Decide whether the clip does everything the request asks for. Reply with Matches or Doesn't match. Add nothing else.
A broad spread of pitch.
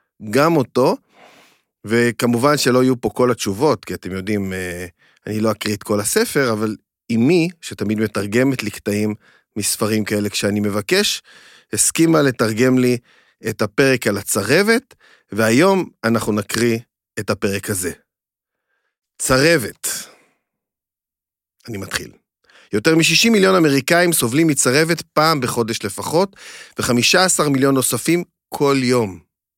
Matches